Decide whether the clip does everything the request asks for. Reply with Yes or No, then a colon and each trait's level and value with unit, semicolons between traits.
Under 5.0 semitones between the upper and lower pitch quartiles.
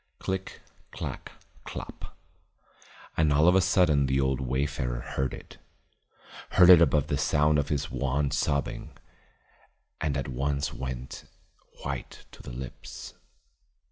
Yes: narrow, 2.4 semitones